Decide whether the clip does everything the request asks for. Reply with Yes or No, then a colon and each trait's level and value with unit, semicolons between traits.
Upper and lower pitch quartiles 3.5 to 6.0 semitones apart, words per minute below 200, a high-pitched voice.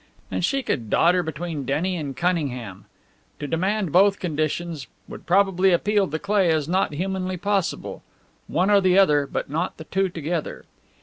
No: average, 3.9 semitones; average, 165 wpm; medium, 175 Hz